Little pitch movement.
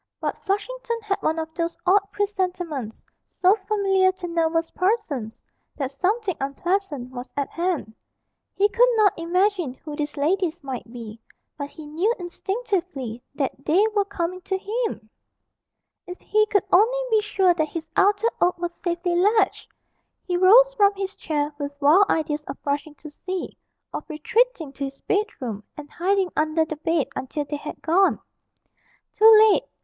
No: average, 5.2 semitones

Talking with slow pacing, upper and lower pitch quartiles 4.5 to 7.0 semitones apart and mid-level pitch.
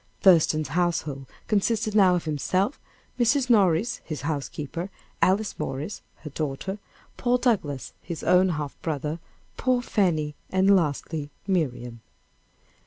Yes: slow, 115 wpm; average, 5.2 semitones; medium, 170 Hz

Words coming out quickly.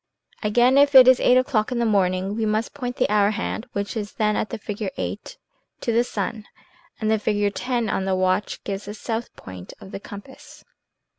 Yes: fast, 210 wpm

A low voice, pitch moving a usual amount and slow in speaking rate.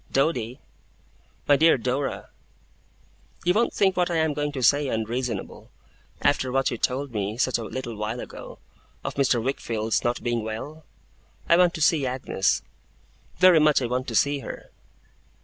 No: low, 130 Hz; average, 4.1 semitones; average, 165 wpm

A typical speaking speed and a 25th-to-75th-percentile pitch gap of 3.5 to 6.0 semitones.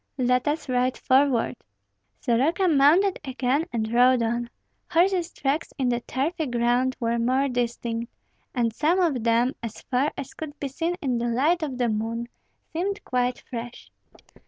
Yes: average, 160 wpm; average, 3.9 semitones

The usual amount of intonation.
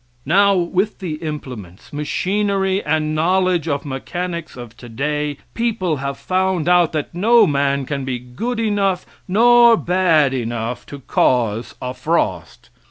No: wide, 5.8 semitones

